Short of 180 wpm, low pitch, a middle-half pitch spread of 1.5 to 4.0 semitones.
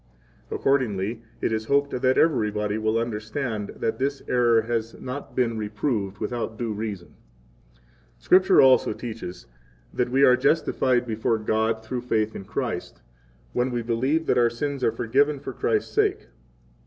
Yes: average, 155 wpm; low, 115 Hz; average, 3.0 semitones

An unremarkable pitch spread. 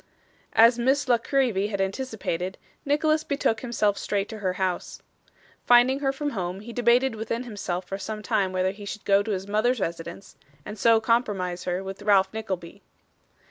Yes: average, 4.1 semitones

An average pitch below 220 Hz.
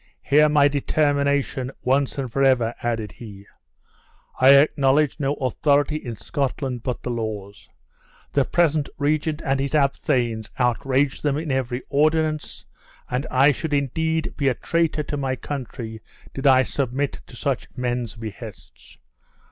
Yes: low, 135 Hz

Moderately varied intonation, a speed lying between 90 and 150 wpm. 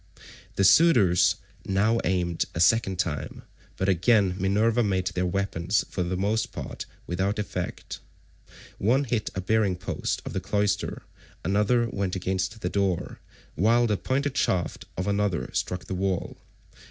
Yes: average, 3.0 semitones; average, 145 wpm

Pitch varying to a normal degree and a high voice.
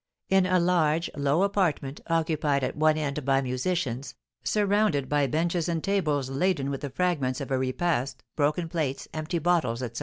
No: average, 4.2 semitones; medium, 155 Hz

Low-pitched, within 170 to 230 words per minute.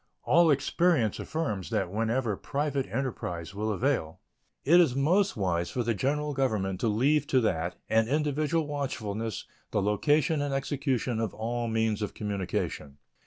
No: low, 120 Hz; average, 150 wpm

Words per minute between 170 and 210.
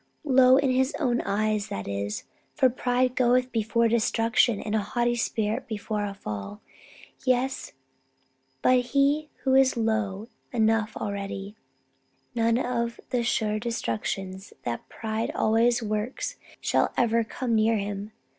No: slow, 135 wpm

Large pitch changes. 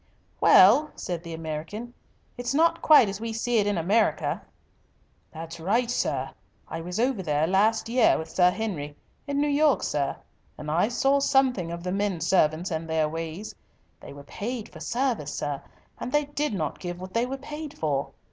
Yes: wide, 7.2 semitones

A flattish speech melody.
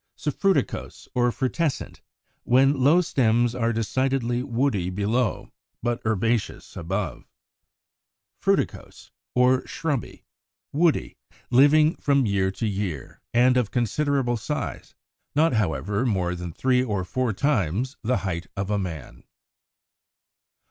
No: average, 4.9 semitones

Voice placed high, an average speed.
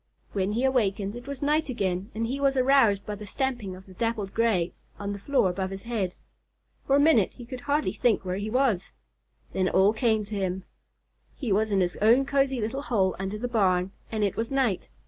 No: high, 215 Hz; fast, 220 wpm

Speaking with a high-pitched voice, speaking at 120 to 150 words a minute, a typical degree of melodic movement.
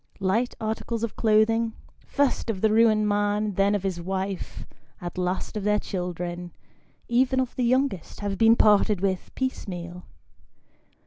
Yes: high, 210 Hz; average, 145 wpm; average, 3.3 semitones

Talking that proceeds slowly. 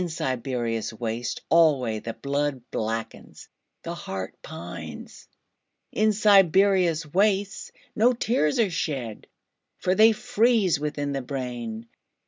Yes: slow, 95 wpm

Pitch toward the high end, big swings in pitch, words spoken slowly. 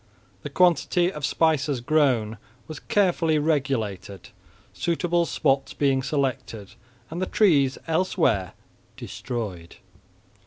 No: medium, 140 Hz; wide, 5.7 semitones; slow, 95 wpm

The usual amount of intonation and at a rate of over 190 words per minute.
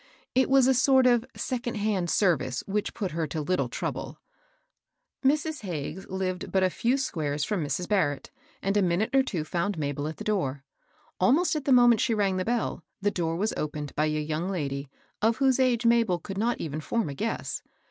No: wide, 7.0 semitones; average, 200 wpm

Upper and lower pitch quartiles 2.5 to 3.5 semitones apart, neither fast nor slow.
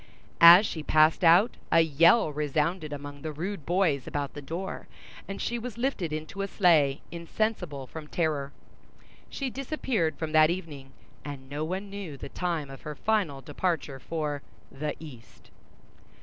No: average, 4.4 semitones; average, 155 wpm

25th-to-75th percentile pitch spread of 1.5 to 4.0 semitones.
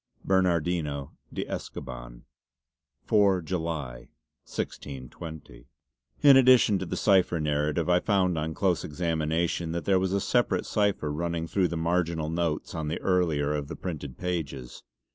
Yes: average, 3.4 semitones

